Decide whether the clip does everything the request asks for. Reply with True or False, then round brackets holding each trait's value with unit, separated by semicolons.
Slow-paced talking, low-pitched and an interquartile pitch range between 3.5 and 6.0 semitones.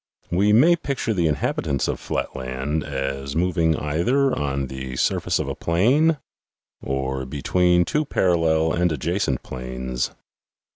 True (130 wpm; 80 Hz; 5.3 semitones)